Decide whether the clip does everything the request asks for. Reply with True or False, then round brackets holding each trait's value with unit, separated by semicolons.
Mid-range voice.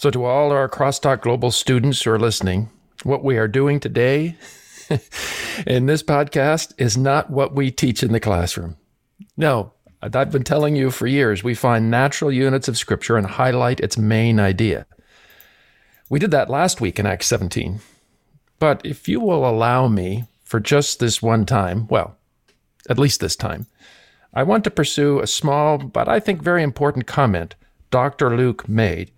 False (125 Hz)